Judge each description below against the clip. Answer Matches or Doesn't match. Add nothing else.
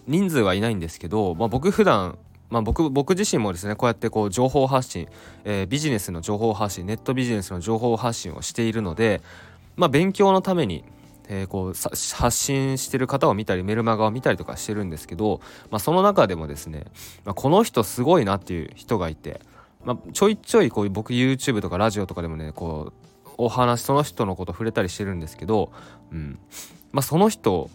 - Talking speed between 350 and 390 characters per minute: Doesn't match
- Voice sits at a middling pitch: Doesn't match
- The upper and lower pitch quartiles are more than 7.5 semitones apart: Doesn't match